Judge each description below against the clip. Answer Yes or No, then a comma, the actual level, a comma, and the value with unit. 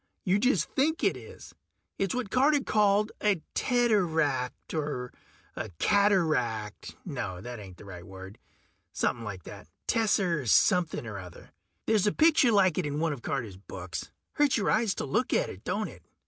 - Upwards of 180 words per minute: No, average, 170 wpm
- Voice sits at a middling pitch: Yes, medium, 165 Hz